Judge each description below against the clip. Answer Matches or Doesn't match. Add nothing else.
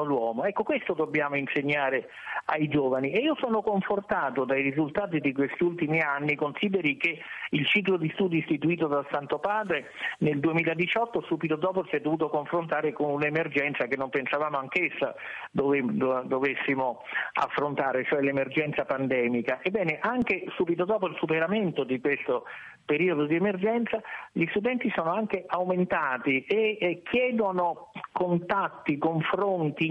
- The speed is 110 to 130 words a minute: Doesn't match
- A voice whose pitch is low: Doesn't match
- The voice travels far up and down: Doesn't match